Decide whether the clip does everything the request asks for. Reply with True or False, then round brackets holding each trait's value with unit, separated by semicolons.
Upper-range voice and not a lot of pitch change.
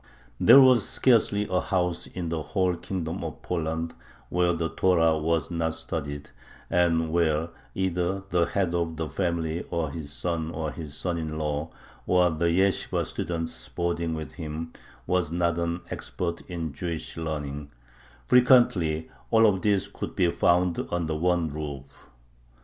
False (85 Hz; 2.0 semitones)